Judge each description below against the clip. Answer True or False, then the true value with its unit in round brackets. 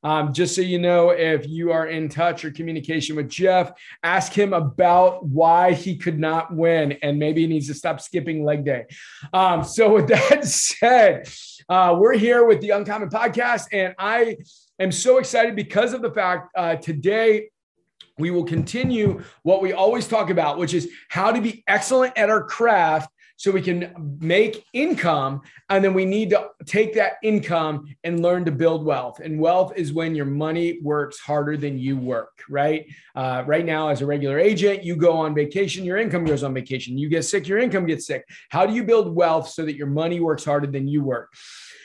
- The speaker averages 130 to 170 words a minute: False (200 wpm)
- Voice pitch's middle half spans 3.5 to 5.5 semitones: True (4.4 semitones)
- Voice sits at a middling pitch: True (170 Hz)